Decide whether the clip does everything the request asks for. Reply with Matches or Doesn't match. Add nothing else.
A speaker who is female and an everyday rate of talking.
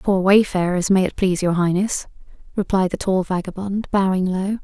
Matches